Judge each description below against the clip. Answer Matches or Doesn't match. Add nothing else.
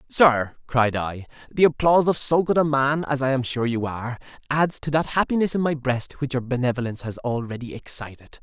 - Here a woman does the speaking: Doesn't match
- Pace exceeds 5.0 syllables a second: Matches